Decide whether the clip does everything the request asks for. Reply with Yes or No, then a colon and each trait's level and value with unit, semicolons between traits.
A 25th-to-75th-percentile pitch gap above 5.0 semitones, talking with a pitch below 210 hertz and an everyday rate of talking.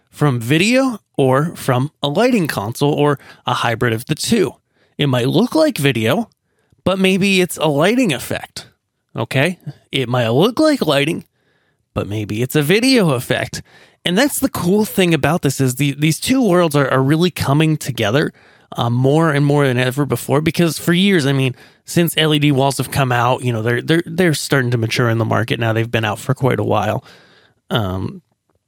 Yes: wide, 5.6 semitones; medium, 140 Hz; average, 190 wpm